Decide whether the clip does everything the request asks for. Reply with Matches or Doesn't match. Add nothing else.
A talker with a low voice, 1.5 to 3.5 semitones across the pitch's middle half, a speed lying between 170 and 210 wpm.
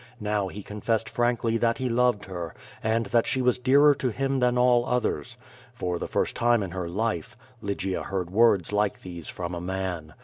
Doesn't match